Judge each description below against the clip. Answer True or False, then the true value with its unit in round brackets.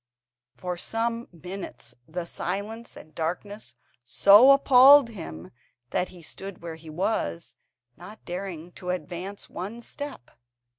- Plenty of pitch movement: False (4.9 semitones)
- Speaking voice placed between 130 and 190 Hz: True (185 Hz)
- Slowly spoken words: True (120 wpm)